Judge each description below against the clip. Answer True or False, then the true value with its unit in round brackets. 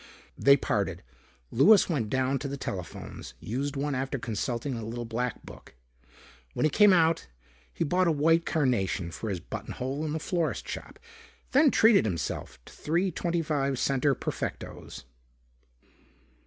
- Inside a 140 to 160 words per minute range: True (155 wpm)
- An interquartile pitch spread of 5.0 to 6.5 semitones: True (5.4 semitones)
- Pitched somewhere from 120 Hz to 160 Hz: True (140 Hz)